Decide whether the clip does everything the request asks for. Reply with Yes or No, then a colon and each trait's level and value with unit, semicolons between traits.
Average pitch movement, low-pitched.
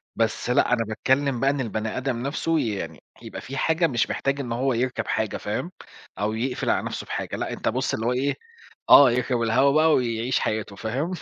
Yes: average, 3.2 semitones; low, 125 Hz